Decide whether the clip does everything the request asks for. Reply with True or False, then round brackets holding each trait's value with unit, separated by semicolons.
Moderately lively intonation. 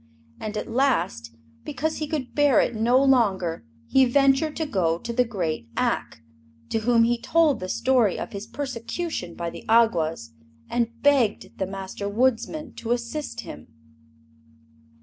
False (5.9 semitones)